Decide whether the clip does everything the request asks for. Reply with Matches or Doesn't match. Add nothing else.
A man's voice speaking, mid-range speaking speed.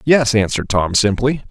Matches